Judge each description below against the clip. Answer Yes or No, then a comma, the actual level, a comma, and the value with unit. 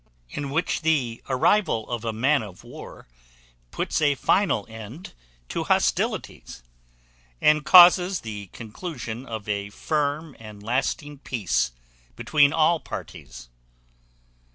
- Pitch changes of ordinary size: No, wide, 5.9 semitones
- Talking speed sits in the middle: No, slow, 115 wpm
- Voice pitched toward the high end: No, low, 130 Hz